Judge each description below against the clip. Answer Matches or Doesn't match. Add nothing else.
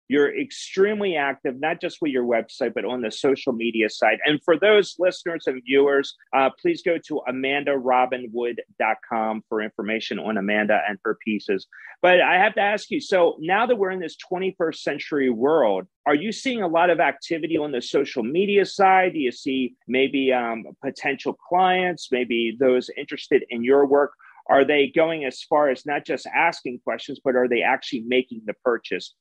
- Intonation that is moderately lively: Doesn't match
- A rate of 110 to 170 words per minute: Doesn't match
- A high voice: Doesn't match